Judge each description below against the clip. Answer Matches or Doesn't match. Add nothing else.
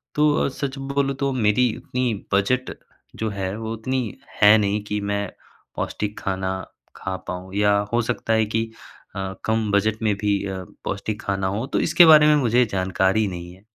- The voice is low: Matches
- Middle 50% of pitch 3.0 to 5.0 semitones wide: Matches